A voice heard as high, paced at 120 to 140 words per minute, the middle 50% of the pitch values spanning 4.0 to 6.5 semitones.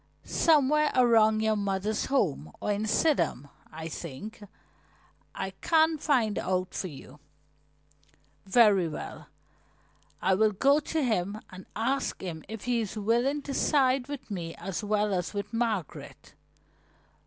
Yes: high, 215 Hz; slow, 135 wpm; wide, 5.4 semitones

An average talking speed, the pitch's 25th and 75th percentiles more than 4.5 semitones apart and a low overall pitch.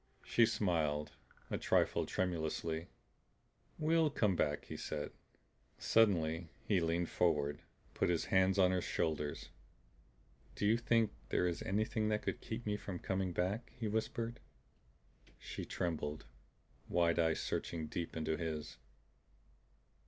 No: slow, 130 wpm; average, 5.0 semitones; very low, 90 Hz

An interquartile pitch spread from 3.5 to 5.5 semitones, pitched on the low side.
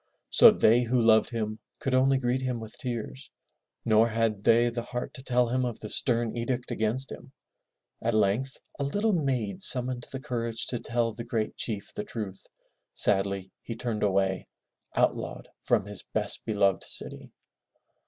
No: average, 2.8 semitones; low, 115 Hz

